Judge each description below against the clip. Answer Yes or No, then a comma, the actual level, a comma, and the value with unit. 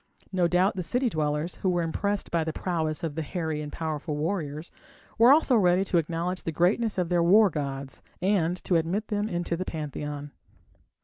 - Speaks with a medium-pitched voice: Yes, medium, 170 Hz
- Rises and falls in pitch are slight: No, average, 3.3 semitones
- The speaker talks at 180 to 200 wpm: Yes, average, 190 wpm